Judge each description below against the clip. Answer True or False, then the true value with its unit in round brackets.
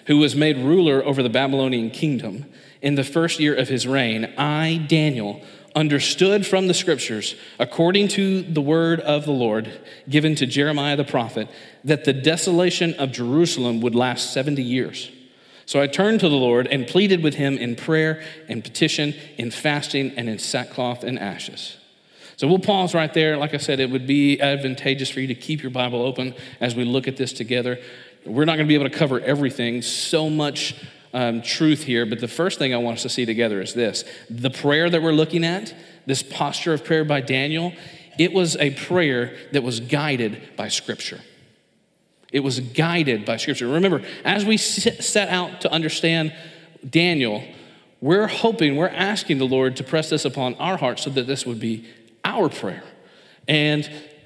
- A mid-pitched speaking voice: True (145 Hz)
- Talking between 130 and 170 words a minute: False (185 wpm)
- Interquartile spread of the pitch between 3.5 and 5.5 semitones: True (4.2 semitones)